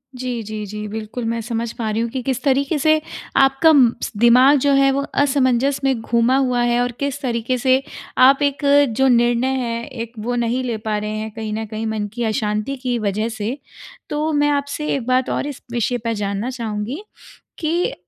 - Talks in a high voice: Yes, high, 245 Hz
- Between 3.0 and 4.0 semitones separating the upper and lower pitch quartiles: Yes, average, 3.4 semitones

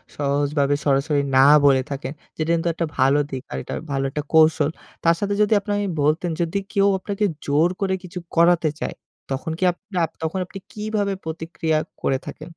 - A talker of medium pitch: Yes, medium, 160 Hz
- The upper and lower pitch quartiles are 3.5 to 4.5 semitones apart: Yes, average, 4.0 semitones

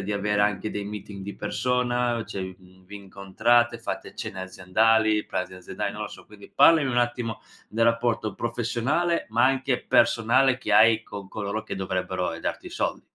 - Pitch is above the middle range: No, low, 110 Hz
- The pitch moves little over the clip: No, average, 3.3 semitones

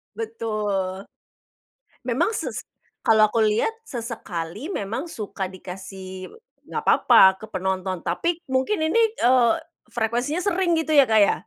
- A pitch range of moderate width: No, wide, 6.5 semitones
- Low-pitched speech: No, high, 225 Hz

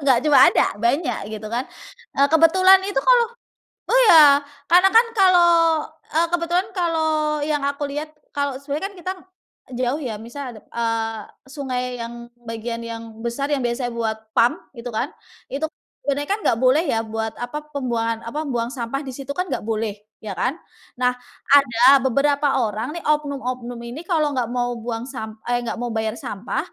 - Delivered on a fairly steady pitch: No, average, 4.5 semitones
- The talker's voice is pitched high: Yes, very high, 265 Hz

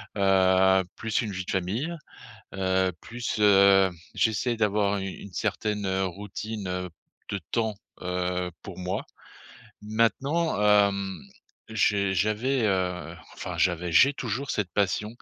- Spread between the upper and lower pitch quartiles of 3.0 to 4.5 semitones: No, narrow, 2.5 semitones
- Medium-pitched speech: No, low, 100 Hz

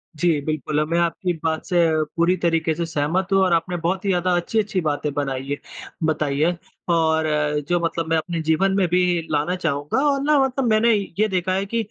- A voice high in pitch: No, medium, 170 Hz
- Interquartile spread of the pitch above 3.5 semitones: No, average, 2.9 semitones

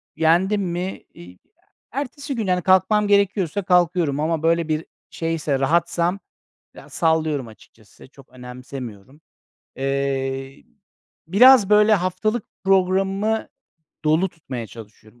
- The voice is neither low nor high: Yes, medium, 170 Hz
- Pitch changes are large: Yes, wide, 6.0 semitones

